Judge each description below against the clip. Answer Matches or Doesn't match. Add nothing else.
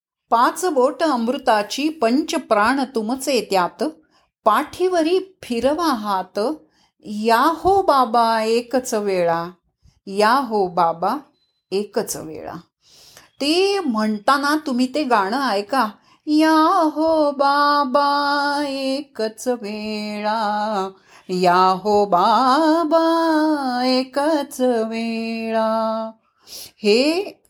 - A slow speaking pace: Matches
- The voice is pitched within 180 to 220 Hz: Doesn't match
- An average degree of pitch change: Doesn't match